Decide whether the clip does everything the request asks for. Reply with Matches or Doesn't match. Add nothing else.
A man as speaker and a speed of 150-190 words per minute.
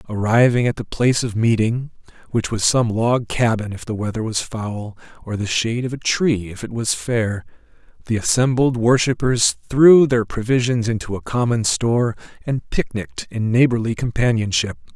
Matches